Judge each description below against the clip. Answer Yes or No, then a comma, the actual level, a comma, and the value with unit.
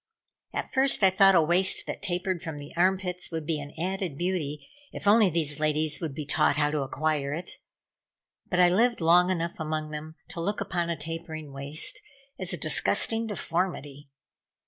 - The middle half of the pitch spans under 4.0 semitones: Yes, average, 3.4 semitones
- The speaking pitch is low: No, medium, 165 Hz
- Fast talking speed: No, average, 185 wpm